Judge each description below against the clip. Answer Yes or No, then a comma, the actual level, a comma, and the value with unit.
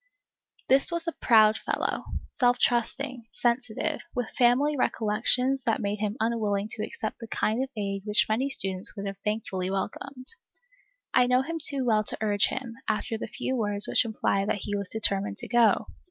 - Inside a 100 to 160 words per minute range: No, average, 180 wpm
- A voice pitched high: Yes, high, 225 Hz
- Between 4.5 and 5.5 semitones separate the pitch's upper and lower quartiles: No, average, 3.3 semitones